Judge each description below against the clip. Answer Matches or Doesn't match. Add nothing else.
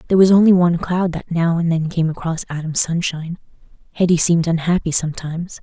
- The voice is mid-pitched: Matches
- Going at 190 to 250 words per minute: Doesn't match